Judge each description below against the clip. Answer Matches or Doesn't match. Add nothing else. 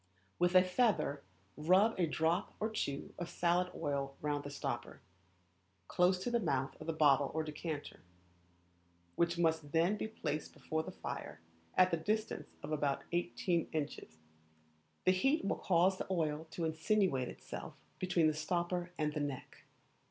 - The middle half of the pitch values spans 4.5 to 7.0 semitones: Doesn't match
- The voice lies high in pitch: Doesn't match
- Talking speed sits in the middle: Matches